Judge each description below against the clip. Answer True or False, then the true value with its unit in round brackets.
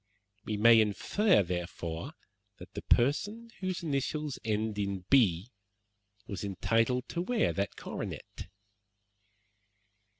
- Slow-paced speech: True (105 wpm)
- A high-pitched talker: False (115 Hz)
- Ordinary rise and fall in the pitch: False (7.3 semitones)